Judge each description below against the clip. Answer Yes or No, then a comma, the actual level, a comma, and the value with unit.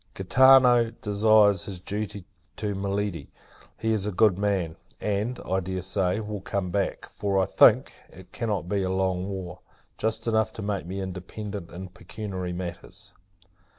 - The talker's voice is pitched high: No, low, 100 Hz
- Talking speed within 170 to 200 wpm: No, average, 155 wpm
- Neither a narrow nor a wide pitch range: No, narrow, 2.3 semitones